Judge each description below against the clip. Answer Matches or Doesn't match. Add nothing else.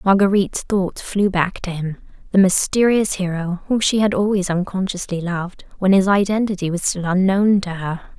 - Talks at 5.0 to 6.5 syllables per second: Matches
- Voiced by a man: Doesn't match